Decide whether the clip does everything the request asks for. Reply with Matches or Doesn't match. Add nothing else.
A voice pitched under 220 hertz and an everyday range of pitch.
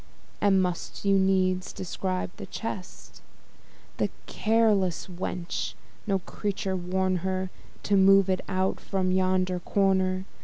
Doesn't match